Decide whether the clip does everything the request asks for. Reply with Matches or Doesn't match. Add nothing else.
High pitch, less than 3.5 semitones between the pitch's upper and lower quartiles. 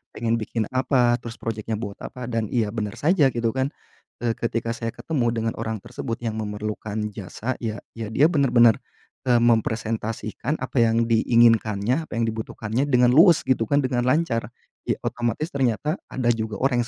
Doesn't match